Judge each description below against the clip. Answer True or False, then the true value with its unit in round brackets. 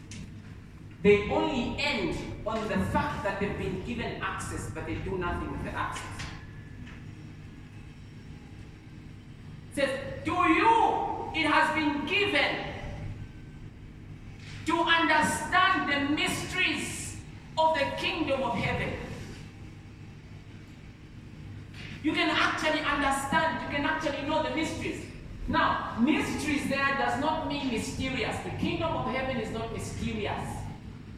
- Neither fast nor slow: False (115 wpm)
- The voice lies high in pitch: True (310 Hz)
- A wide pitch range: False (3.2 semitones)